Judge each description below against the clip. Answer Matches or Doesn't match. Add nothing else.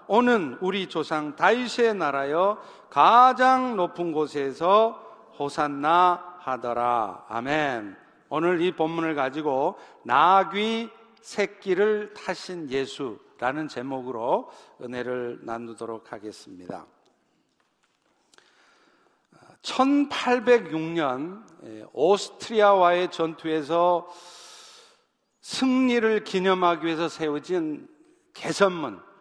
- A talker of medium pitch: Matches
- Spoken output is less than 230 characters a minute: Matches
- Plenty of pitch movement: Matches